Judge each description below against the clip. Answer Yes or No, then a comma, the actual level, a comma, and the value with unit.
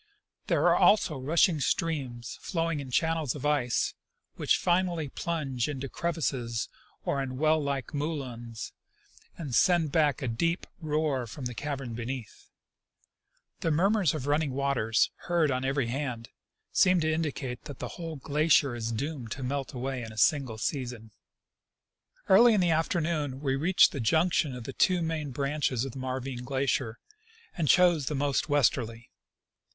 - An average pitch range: Yes, average, 4.1 semitones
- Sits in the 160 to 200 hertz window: No, medium, 140 Hz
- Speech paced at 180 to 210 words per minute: No, average, 155 wpm